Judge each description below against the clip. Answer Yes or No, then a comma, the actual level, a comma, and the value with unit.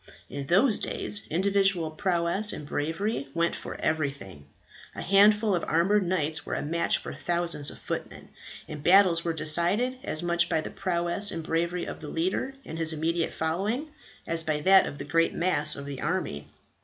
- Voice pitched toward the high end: No, medium, 170 Hz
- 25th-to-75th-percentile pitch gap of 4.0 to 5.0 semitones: No, average, 3.6 semitones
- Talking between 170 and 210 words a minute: Yes, average, 180 wpm